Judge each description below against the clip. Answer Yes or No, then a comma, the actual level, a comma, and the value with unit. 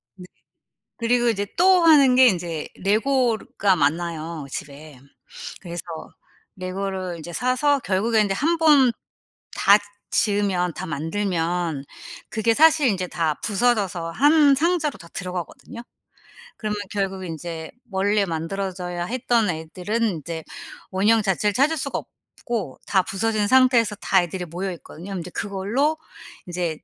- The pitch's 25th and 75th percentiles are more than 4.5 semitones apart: Yes, wide, 5.4 semitones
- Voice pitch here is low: No, high, 195 Hz